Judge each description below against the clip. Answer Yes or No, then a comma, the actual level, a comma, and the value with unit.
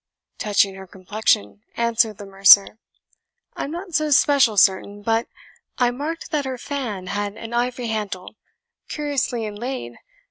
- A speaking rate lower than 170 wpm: Yes, average, 140 wpm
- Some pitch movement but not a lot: Yes, average, 4.8 semitones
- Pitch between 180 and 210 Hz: No, high, 225 Hz